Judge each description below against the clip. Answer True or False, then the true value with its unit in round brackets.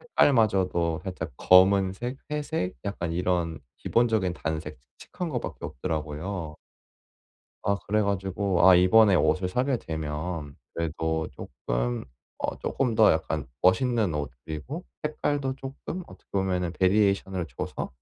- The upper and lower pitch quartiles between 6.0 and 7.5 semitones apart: False (5.1 semitones)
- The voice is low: True (95 Hz)